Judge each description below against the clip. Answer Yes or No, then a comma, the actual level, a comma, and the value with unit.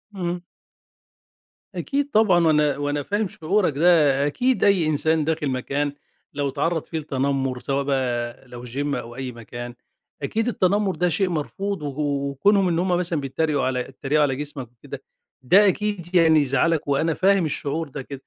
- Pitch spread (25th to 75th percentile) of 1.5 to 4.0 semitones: No, average, 4.6 semitones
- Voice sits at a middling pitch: Yes, medium, 150 Hz